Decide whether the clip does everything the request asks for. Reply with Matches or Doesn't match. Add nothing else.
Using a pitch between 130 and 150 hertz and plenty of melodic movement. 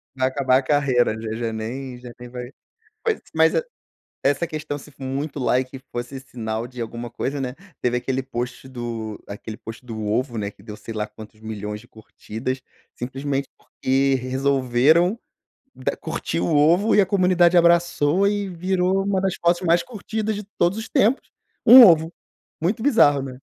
Matches